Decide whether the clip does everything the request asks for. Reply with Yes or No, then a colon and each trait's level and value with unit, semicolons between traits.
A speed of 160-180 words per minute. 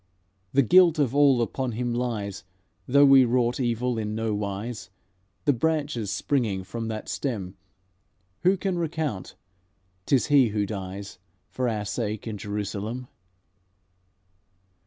No: slow, 135 wpm